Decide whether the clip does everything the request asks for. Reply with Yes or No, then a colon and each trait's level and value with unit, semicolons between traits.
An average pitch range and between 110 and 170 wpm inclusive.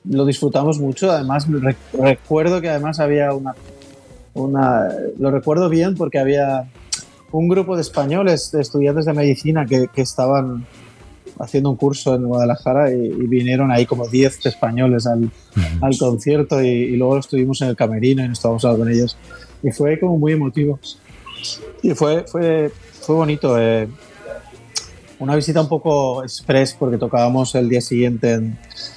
Yes: average, 3.3 semitones; average, 155 wpm